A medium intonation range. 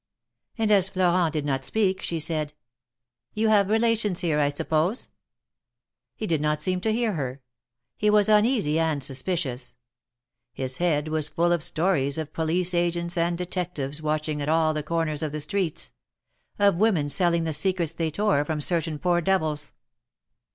Yes: average, 3.7 semitones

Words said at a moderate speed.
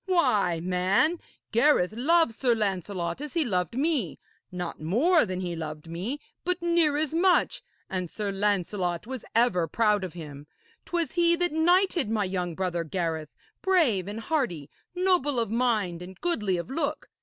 Yes: average, 160 wpm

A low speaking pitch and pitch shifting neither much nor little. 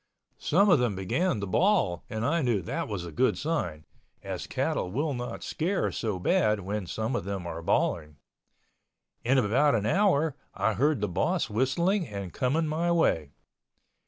No: low, 120 Hz; wide, 8.2 semitones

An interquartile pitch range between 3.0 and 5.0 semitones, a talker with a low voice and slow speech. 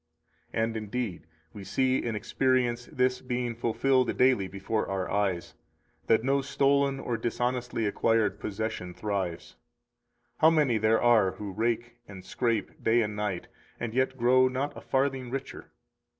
No: average, 3.5 semitones; low, 120 Hz; average, 150 wpm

